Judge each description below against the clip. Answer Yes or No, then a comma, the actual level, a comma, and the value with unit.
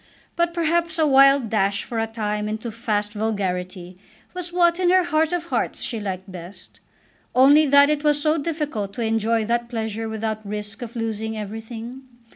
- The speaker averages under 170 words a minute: No, average, 175 wpm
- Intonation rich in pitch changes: Yes, wide, 6.0 semitones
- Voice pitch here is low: No, high, 225 Hz